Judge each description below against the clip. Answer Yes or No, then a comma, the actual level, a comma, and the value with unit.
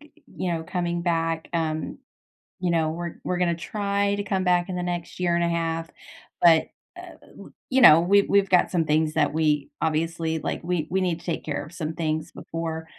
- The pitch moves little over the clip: Yes, narrow, 1.9 semitones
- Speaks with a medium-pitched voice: Yes, medium, 170 Hz